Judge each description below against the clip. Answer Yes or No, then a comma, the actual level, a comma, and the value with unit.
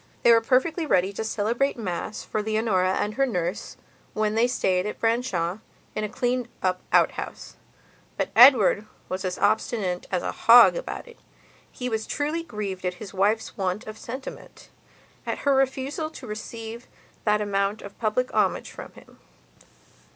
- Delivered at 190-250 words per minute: No, average, 160 wpm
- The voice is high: Yes, high, 220 Hz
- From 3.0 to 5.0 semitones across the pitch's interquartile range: Yes, average, 4.0 semitones